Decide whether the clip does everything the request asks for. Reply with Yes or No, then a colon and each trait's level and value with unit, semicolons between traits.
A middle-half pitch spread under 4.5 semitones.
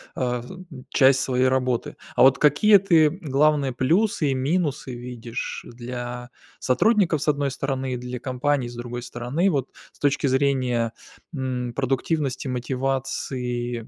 Yes: average, 2.8 semitones